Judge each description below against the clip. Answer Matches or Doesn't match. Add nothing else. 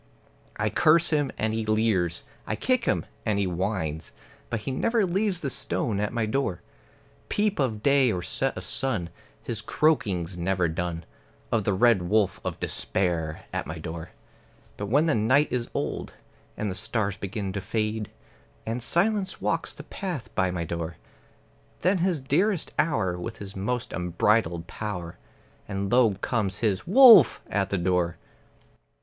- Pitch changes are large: Matches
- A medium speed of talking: Matches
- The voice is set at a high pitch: Doesn't match